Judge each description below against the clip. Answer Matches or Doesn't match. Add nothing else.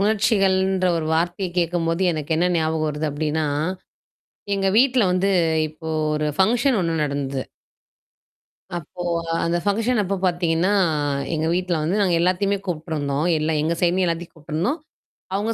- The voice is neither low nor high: Matches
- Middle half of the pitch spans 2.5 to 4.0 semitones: Matches